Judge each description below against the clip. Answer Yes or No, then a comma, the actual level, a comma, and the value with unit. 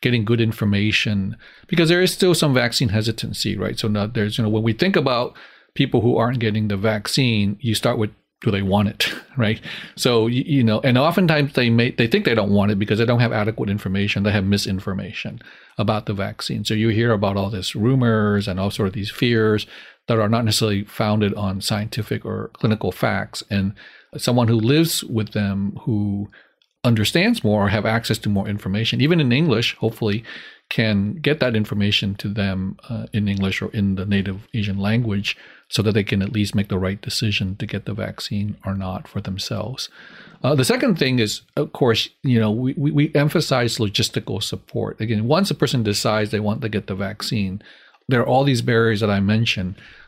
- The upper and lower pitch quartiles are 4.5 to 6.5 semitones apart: No, average, 2.9 semitones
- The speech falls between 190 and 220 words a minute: Yes, average, 200 wpm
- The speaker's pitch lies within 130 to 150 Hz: No, low, 110 Hz